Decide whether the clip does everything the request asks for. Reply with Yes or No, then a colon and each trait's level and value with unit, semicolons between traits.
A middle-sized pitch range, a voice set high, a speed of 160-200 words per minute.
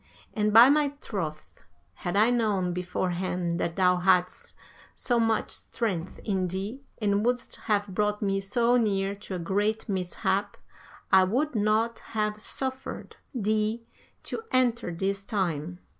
No: average, 3.4 semitones; high, 205 Hz; average, 140 wpm